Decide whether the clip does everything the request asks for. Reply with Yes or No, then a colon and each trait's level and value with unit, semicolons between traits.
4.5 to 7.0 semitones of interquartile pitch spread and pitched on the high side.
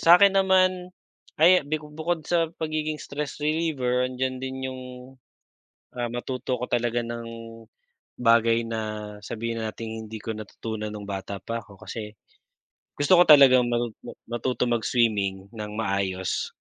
No: average, 5.1 semitones; low, 120 Hz